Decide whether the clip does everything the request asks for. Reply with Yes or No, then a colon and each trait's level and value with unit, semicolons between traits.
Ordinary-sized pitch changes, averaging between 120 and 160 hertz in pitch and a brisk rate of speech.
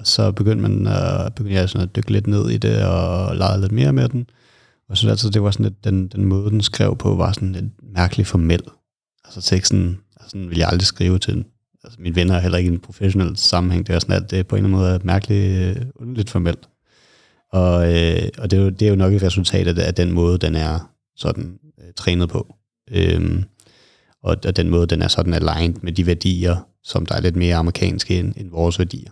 No: average, 3.1 semitones; very low, 95 Hz; fast, 235 wpm